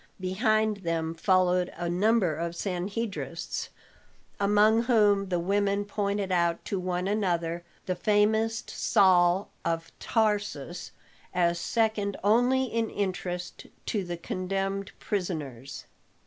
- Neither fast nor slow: No, slow, 110 wpm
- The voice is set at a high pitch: Yes, high, 195 Hz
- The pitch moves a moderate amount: Yes, average, 3.1 semitones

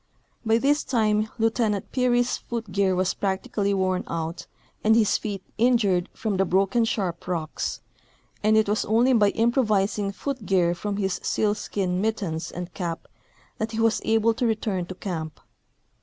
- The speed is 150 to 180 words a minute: Yes, average, 165 wpm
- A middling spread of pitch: Yes, average, 3.3 semitones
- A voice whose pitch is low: No, high, 205 Hz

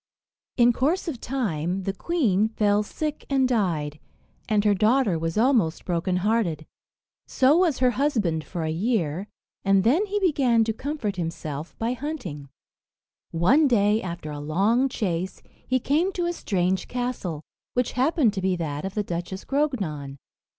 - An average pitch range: No, wide, 7.0 semitones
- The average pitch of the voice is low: No, high, 210 Hz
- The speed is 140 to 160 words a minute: Yes, average, 155 wpm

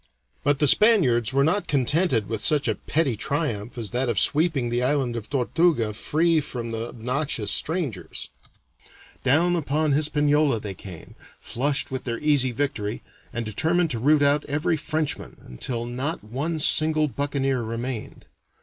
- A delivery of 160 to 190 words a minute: No, average, 150 wpm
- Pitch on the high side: No, medium, 140 Hz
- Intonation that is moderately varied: Yes, average, 4.6 semitones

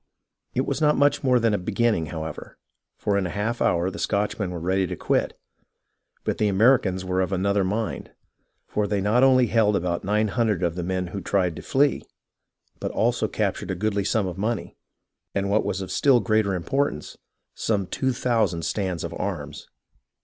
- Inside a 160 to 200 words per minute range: Yes, average, 190 wpm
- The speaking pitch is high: No, low, 100 Hz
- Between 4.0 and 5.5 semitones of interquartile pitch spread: No, average, 3.5 semitones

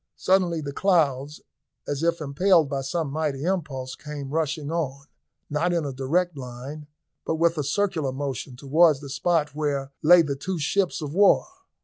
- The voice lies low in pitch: No, medium, 150 Hz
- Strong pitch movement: No, average, 3.4 semitones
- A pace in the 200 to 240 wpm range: No, average, 165 wpm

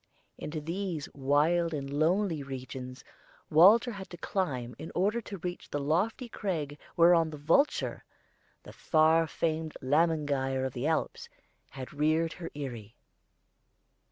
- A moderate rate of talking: No, slow, 130 wpm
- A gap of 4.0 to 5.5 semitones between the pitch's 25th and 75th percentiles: No, average, 3.6 semitones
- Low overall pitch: No, medium, 155 Hz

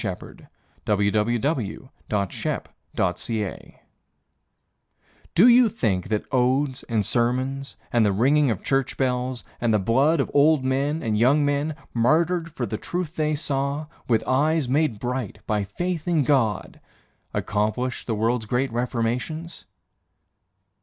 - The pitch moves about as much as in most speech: Yes, average, 4.7 semitones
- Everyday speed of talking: No, slow, 125 wpm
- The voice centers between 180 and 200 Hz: No, low, 130 Hz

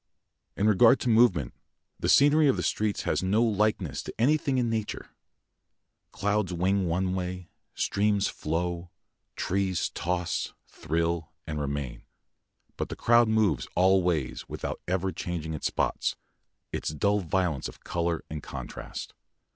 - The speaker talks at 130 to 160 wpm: Yes, average, 140 wpm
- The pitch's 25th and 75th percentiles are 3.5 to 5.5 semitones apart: Yes, average, 4.2 semitones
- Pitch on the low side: Yes, very low, 95 Hz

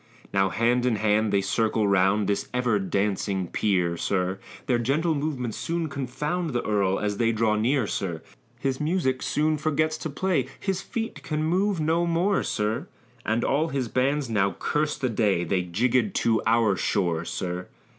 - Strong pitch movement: Yes, wide, 7.0 semitones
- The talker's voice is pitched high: No, low, 115 Hz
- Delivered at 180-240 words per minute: No, average, 170 wpm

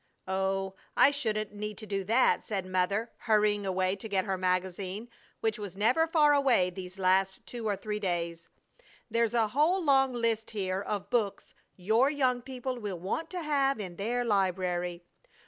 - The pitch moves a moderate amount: Yes, average, 4.4 semitones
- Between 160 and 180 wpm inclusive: Yes, average, 170 wpm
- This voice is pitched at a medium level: No, high, 210 Hz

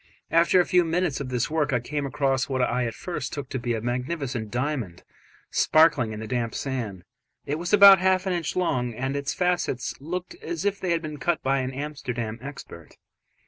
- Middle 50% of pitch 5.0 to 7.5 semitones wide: Yes, wide, 5.5 semitones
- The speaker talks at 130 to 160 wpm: No, fast, 205 wpm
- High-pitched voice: No, medium, 140 Hz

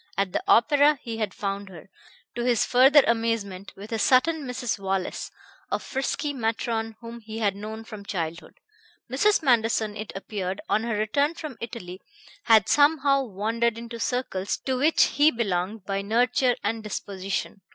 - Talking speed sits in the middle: Yes, average, 160 wpm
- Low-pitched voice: No, high, 225 Hz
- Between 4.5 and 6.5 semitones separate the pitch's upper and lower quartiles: No, average, 4.0 semitones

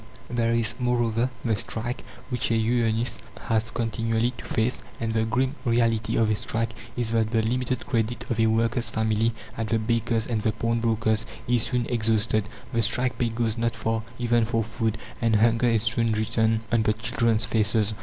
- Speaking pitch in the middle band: No, low, 115 Hz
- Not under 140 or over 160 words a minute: No, average, 185 wpm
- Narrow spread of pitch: Yes, narrow, 1.0 semitones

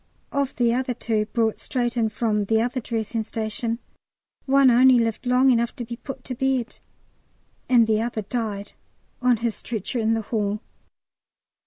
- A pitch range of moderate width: No, narrow, 2.2 semitones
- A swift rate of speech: No, average, 165 wpm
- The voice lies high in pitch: Yes, high, 235 Hz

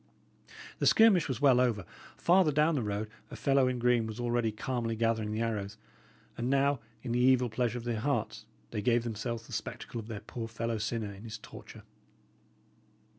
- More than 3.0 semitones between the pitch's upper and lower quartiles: No, narrow, 2.5 semitones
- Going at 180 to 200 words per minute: Yes, average, 185 wpm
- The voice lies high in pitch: No, low, 120 Hz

